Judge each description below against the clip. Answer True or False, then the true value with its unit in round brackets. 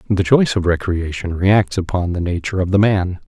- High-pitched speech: False (95 Hz)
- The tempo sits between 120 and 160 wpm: False (200 wpm)